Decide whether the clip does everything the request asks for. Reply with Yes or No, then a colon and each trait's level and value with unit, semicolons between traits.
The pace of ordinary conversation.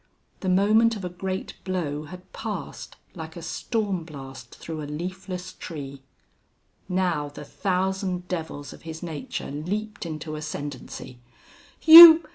No: slow, 130 wpm